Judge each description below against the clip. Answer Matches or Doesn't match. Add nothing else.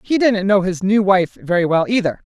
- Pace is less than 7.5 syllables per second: Matches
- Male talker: Doesn't match